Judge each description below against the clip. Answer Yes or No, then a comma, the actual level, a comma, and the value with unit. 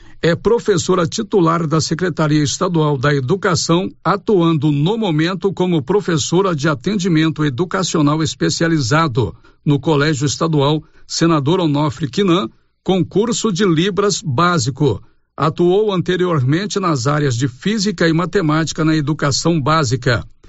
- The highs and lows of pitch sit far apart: No, average, 3.6 semitones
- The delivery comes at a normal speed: No, slow, 110 wpm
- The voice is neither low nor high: Yes, medium, 165 Hz